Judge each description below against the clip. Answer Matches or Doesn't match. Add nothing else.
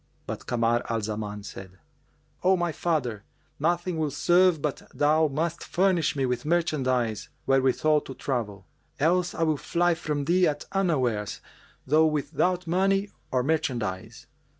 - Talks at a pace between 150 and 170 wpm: Doesn't match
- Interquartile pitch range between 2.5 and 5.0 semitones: Doesn't match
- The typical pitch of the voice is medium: Matches